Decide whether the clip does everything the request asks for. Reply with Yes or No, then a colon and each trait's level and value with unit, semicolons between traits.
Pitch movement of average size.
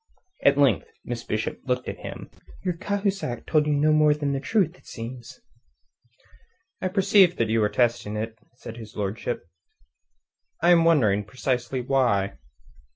No: wide, 6.4 semitones